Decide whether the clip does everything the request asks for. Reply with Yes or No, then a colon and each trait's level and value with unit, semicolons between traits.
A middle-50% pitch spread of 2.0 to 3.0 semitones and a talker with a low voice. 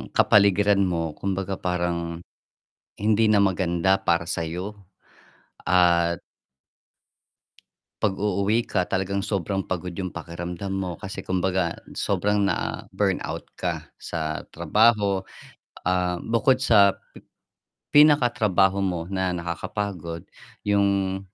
Yes: narrow, 2.6 semitones; very low, 95 Hz